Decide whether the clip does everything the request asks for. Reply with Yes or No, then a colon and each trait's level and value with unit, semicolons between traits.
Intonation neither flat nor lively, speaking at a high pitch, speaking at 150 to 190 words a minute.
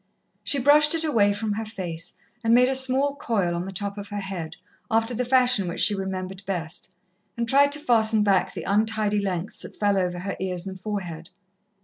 No: average, 3.9 semitones; high, 205 Hz; fast, 205 wpm